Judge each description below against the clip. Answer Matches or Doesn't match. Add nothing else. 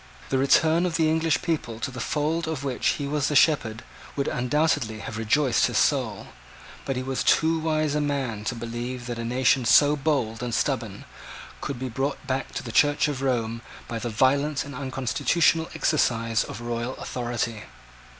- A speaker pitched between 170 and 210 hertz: Doesn't match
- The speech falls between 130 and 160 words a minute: Doesn't match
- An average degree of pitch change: Matches